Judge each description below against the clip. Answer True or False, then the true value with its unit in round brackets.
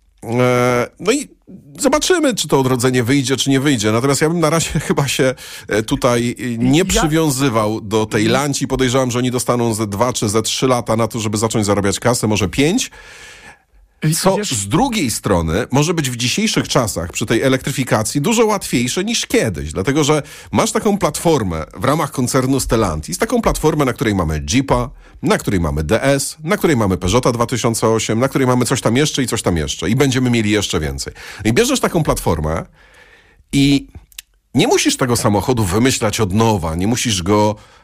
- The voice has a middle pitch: False (125 Hz)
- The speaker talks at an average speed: False (175 wpm)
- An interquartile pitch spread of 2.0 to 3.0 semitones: False (4.9 semitones)